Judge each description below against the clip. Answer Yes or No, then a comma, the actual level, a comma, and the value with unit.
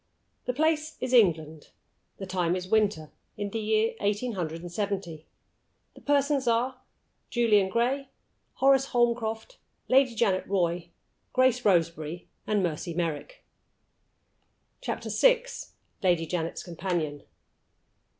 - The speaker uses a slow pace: Yes, slow, 115 wpm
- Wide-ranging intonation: Yes, wide, 6.4 semitones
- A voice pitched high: Yes, high, 205 Hz